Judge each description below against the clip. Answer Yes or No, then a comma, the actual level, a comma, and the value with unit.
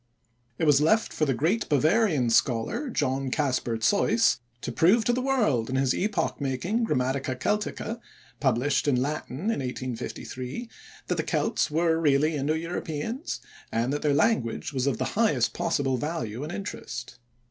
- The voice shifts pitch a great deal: Yes, wide, 6.6 semitones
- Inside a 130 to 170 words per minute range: Yes, average, 160 wpm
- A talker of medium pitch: Yes, medium, 145 Hz